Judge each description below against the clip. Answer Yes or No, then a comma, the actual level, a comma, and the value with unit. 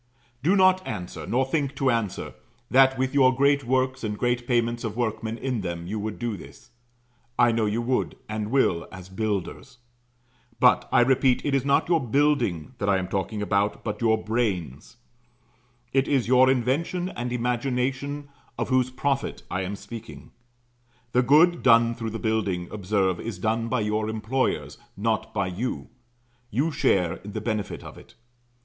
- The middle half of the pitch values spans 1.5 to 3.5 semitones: No, average, 3.9 semitones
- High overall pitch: No, low, 120 Hz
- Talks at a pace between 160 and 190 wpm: Yes, average, 170 wpm